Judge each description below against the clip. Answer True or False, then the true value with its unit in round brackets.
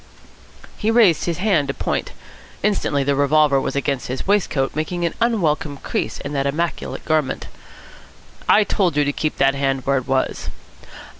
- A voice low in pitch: False (150 Hz)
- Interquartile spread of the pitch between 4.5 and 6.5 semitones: False (4.0 semitones)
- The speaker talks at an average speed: True (165 wpm)